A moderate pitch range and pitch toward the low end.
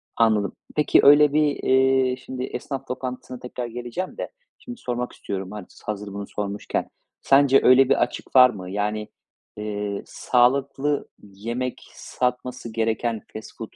Yes: average, 3.8 semitones; low, 125 Hz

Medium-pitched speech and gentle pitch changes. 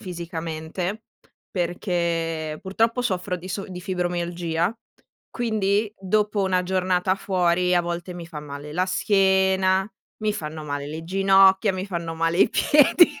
Yes: medium, 180 Hz; narrow, 2.3 semitones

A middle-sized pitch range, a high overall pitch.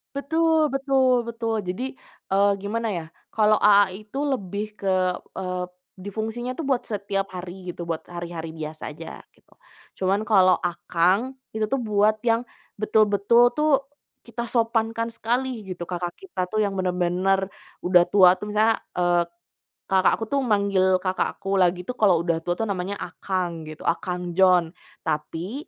Yes: average, 4.1 semitones; high, 200 Hz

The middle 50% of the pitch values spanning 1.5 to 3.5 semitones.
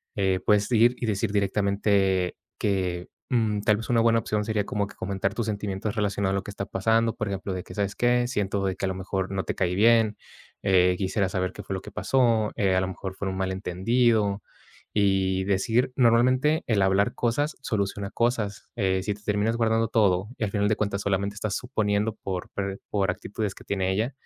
Yes: average, 2.7 semitones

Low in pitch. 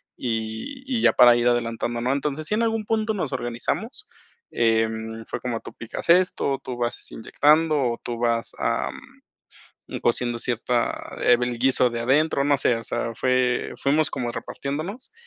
Yes: low, 125 Hz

